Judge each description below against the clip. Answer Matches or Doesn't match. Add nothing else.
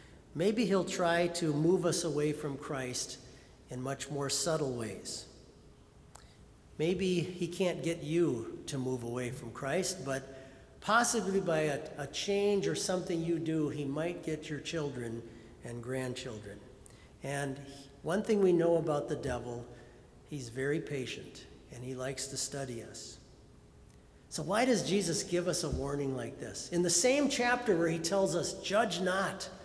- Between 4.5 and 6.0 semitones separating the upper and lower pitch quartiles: Matches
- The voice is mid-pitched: Matches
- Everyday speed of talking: Matches